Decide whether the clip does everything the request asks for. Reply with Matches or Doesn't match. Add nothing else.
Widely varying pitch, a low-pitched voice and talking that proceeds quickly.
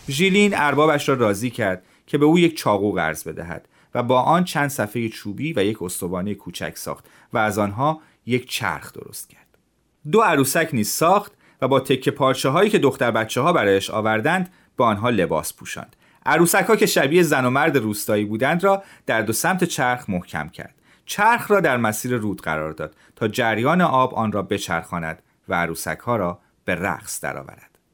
Matches